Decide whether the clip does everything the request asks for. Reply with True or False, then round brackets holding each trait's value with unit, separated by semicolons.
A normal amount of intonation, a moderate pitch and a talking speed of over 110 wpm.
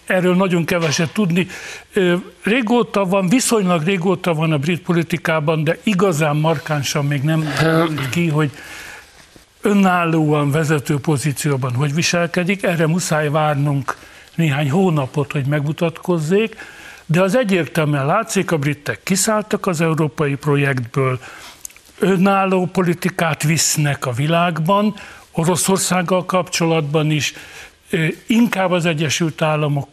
False (3.6 semitones; 165 Hz; 105 wpm)